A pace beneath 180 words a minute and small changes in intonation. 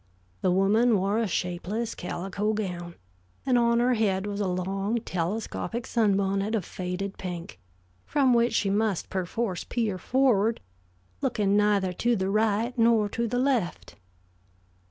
No: average, 140 wpm; average, 3.5 semitones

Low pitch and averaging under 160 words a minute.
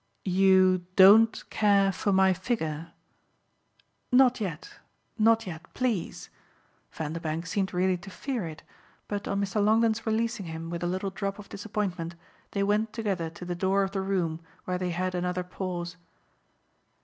No: high, 190 Hz; average, 150 wpm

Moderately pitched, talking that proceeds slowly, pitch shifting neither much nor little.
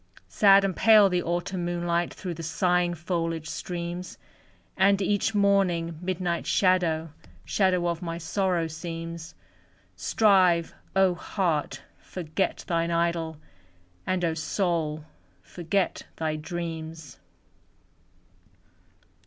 No: medium, 175 Hz; slow, 105 wpm; narrow, 2.1 semitones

